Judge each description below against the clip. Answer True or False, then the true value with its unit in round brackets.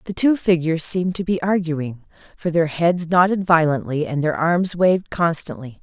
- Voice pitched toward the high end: False (170 Hz)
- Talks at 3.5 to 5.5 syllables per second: True (5.0 syllables/s)